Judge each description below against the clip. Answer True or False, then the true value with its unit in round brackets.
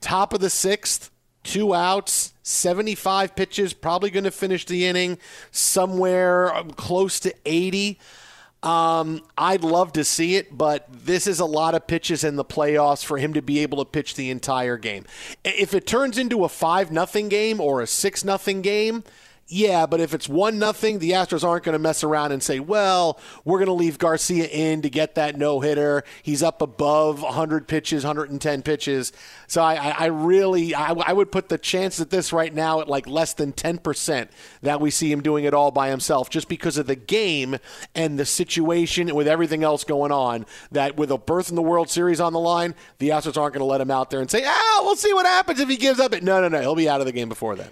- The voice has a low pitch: False (165 Hz)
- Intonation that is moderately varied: True (3.9 semitones)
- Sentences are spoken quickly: True (225 wpm)